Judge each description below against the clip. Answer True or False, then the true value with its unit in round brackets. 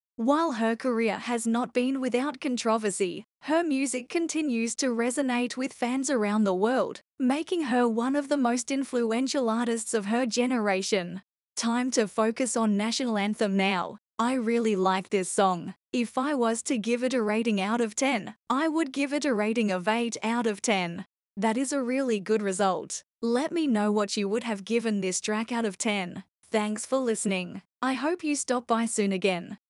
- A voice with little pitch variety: False (3.5 semitones)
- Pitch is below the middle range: False (230 Hz)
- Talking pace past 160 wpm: True (185 wpm)